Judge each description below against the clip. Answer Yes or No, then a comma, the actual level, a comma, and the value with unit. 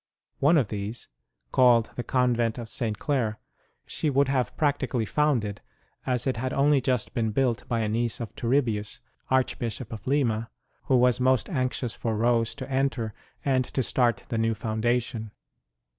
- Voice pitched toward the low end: Yes, low, 120 Hz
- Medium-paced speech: Yes, average, 165 wpm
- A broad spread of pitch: No, average, 2.7 semitones